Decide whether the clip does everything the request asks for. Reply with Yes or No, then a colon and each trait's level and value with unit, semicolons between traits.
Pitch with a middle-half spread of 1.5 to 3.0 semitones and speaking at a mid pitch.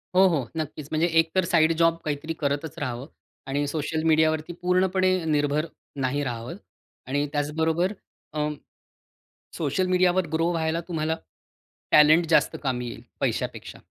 Yes: narrow, 2.5 semitones; medium, 155 Hz